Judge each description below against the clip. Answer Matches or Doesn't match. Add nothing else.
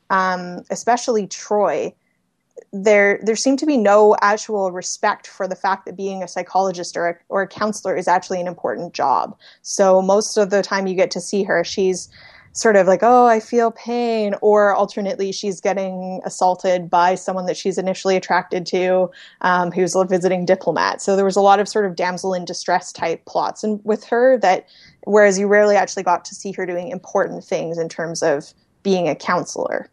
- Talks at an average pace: Matches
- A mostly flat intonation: Matches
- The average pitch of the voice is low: Doesn't match